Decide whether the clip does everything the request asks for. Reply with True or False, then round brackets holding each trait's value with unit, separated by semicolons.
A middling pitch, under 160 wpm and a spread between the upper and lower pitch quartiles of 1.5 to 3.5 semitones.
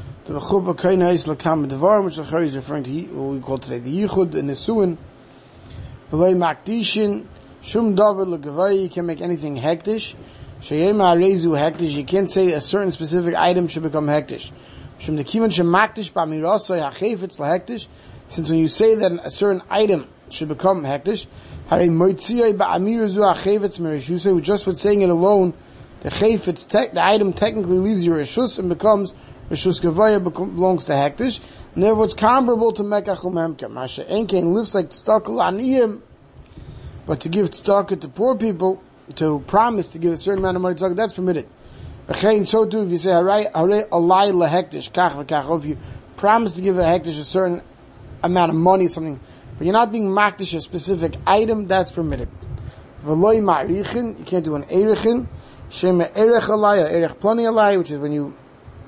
False (180 Hz; 145 wpm; 4.3 semitones)